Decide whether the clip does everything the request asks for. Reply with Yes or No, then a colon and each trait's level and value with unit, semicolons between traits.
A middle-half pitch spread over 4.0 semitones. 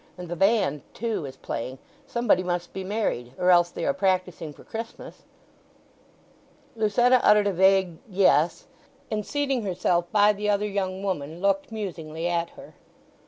No: average, 3.4 semitones